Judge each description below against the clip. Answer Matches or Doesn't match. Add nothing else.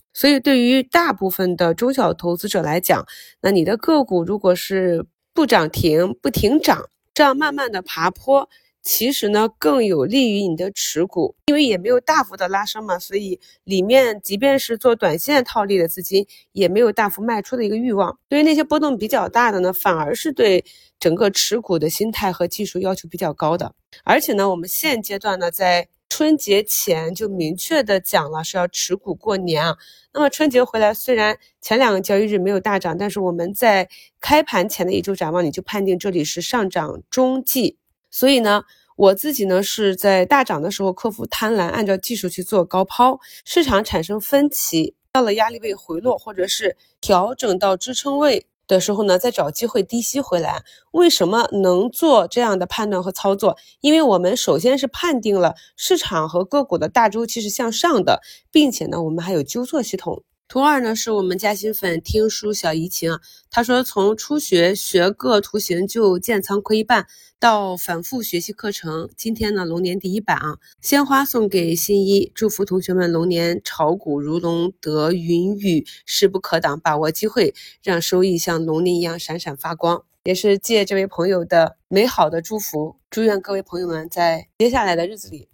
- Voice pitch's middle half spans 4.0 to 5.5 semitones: Matches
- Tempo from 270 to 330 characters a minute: Matches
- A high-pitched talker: Matches